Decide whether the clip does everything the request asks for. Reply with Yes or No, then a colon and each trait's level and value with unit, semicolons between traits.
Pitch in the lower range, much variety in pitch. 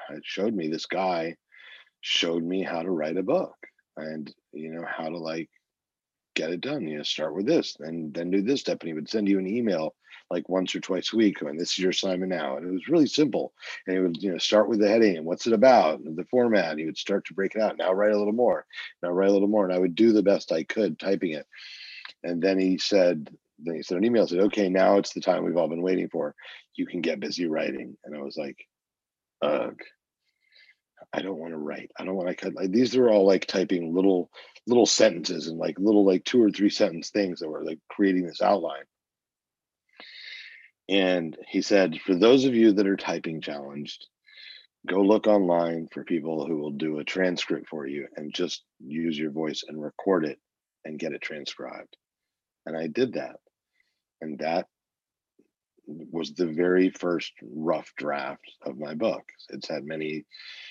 No: very low, 90 Hz; average, 3.4 semitones